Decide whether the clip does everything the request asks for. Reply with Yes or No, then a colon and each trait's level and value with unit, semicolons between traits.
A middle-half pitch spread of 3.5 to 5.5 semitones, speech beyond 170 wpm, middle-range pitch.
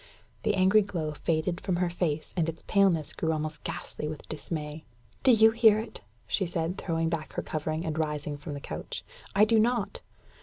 Yes: average, 4.2 semitones; average, 190 wpm; medium, 165 Hz